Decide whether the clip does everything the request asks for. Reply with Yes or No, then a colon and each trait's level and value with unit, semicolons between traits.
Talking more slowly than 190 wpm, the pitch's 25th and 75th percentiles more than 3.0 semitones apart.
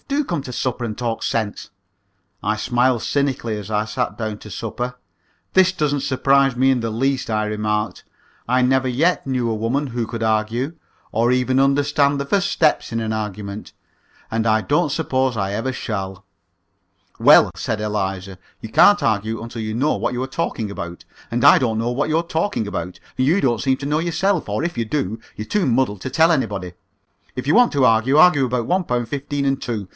No: average, 200 wpm; average, 4.3 semitones